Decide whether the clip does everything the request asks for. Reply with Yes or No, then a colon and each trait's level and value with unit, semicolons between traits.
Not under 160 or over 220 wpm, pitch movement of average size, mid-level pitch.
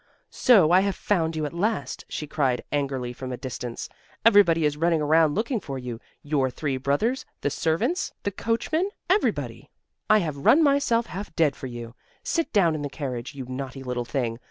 No: average, 185 wpm; wide, 7.4 semitones; medium, 155 Hz